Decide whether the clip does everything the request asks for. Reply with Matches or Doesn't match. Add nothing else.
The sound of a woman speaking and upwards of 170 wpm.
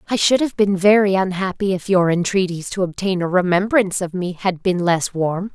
Matches